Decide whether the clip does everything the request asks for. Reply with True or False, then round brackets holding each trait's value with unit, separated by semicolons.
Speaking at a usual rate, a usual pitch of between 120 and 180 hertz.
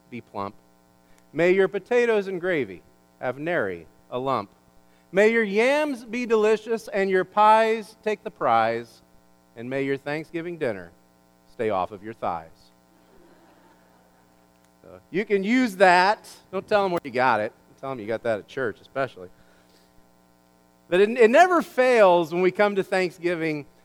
True (155 wpm; 135 Hz)